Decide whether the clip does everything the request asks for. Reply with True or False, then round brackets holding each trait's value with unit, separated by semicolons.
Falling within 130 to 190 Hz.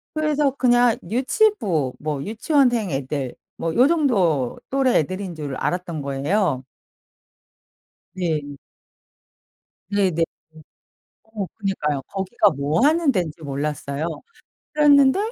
True (185 Hz)